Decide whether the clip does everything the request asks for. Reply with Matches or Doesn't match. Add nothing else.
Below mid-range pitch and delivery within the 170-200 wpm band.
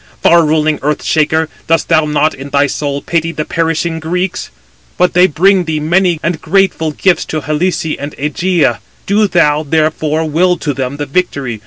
Doesn't match